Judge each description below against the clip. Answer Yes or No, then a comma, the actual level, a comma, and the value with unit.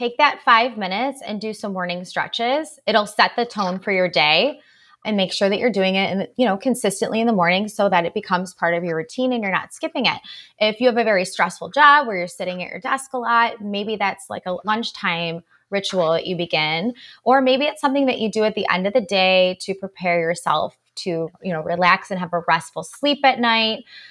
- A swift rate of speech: Yes, fast, 235 wpm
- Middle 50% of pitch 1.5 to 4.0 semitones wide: No, average, 5.1 semitones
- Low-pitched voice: No, high, 200 Hz